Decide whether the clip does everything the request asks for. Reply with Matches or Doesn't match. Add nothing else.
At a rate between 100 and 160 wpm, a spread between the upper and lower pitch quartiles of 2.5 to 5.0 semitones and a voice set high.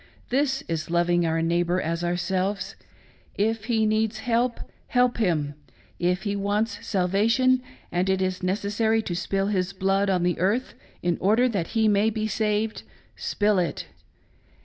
Matches